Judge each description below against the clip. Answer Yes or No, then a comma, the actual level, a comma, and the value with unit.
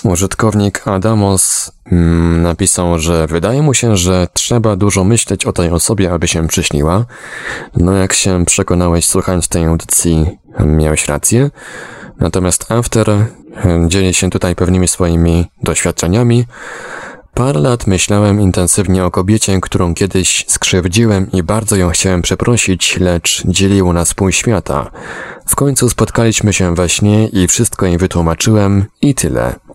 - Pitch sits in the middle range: No, very low, 95 Hz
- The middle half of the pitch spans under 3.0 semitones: No, average, 3.5 semitones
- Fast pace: No, average, 130 wpm